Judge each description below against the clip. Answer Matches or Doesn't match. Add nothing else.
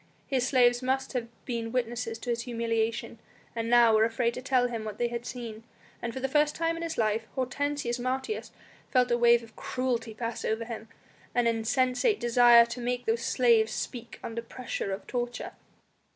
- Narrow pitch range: Matches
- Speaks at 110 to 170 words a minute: Doesn't match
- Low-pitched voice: Doesn't match